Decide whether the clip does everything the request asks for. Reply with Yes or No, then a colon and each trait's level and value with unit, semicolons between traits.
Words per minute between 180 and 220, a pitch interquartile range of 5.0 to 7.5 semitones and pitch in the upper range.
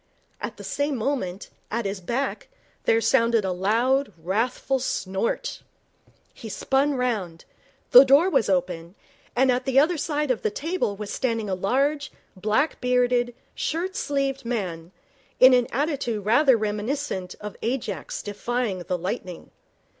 No: average, 140 wpm; average, 5.3 semitones; high, 235 Hz